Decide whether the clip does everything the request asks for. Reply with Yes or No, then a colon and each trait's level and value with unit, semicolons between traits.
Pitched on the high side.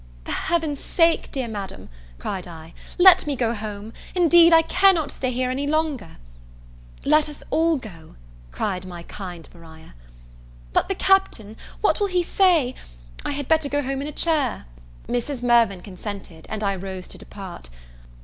Yes: very high, 255 Hz